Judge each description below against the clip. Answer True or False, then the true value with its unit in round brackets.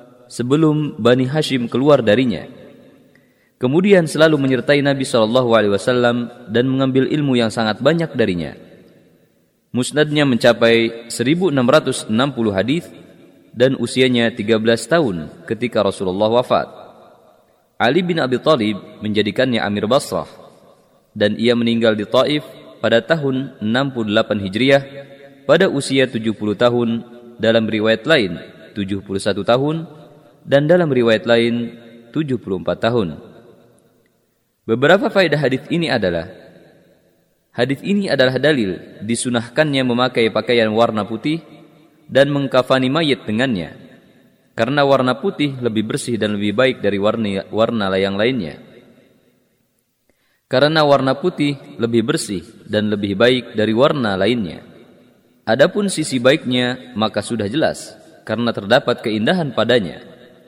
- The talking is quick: False (110 wpm)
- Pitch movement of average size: True (3.8 semitones)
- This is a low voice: True (120 Hz)